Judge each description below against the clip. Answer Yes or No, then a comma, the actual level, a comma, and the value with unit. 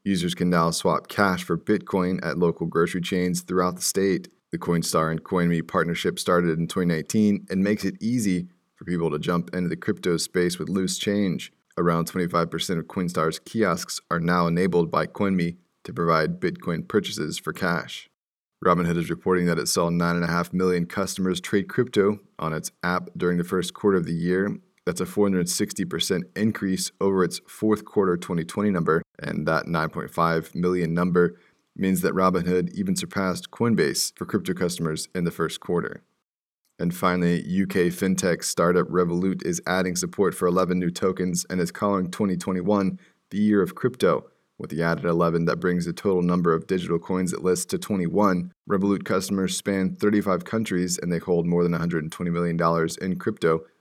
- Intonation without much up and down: Yes, narrow, 1.6 semitones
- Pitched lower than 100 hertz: Yes, very low, 90 Hz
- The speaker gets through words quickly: No, average, 170 wpm